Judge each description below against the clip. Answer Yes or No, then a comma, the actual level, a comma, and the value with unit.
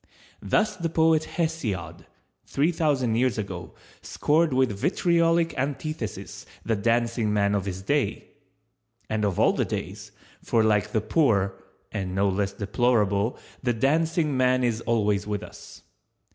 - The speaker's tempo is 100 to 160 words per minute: Yes, average, 140 wpm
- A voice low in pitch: Yes, low, 115 Hz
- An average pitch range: No, wide, 6.9 semitones